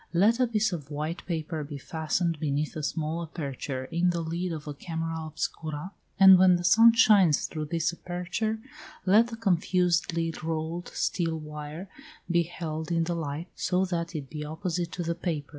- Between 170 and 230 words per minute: Yes, average, 175 wpm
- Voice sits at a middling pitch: Yes, medium, 165 Hz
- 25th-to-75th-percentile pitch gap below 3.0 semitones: Yes, narrow, 2.4 semitones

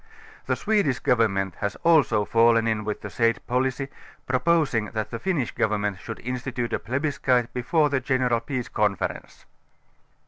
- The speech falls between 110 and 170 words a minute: Yes, average, 145 wpm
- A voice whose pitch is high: No, low, 120 Hz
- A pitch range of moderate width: Yes, average, 3.4 semitones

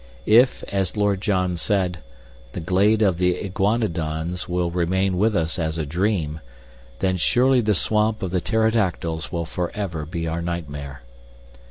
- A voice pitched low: Yes, very low, 90 Hz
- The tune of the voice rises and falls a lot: No, average, 3.7 semitones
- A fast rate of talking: No, average, 150 wpm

